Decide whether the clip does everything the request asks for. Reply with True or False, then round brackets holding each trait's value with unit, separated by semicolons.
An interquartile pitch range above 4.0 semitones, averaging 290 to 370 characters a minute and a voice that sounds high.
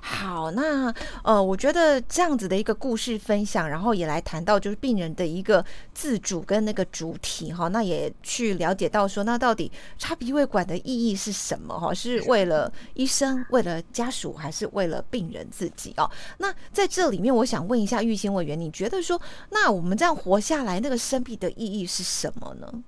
True (5.2 semitones; 300 characters per minute; 220 Hz)